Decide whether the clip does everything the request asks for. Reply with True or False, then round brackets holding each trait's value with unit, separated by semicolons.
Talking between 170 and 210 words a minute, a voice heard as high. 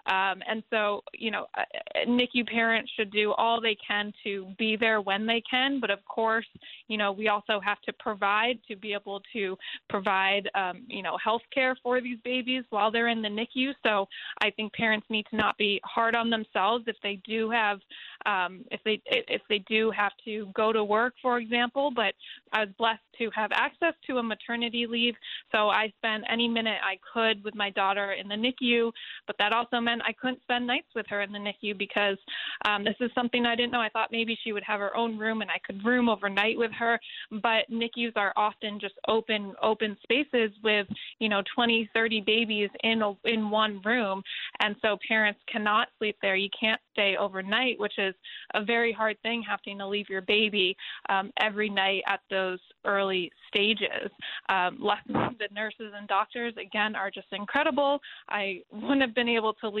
True (200 wpm; 220 Hz)